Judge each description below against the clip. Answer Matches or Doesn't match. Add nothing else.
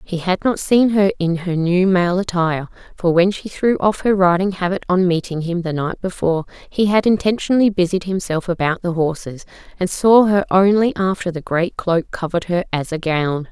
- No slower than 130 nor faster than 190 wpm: Doesn't match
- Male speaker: Doesn't match